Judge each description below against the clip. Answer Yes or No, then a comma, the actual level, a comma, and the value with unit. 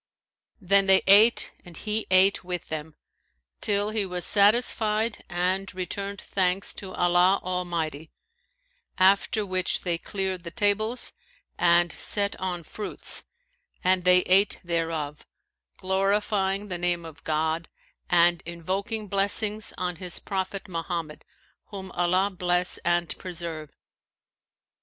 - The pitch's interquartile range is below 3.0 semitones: Yes, narrow, 2.5 semitones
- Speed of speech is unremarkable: No, slow, 120 wpm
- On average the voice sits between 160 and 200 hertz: Yes, medium, 185 Hz